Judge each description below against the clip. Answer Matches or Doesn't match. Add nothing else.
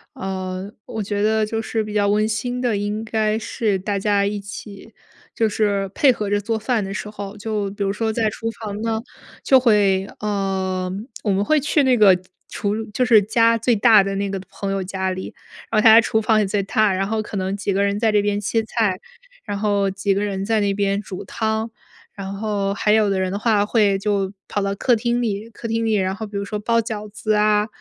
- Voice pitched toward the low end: Doesn't match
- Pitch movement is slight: Matches